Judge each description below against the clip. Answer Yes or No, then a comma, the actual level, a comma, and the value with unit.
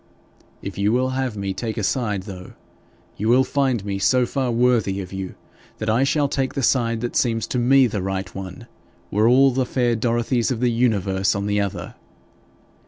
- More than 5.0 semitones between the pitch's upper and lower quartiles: No, average, 4.1 semitones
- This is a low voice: Yes, low, 115 Hz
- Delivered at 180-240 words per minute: Yes, average, 195 wpm